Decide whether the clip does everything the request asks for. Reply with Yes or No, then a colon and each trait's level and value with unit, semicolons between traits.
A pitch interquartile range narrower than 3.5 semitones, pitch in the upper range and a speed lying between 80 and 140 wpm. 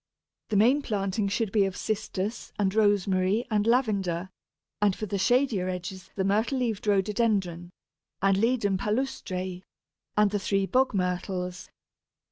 Yes: average, 2.7 semitones; high, 200 Hz; slow, 135 wpm